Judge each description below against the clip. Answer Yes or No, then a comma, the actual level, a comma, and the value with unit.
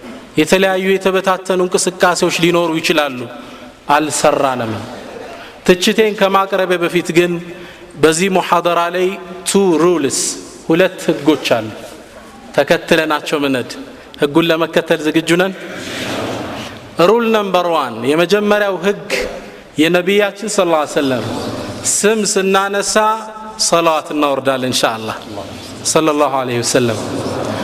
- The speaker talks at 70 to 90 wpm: Yes, average, 85 wpm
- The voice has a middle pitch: Yes, medium, 175 Hz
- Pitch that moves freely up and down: No, average, 4.3 semitones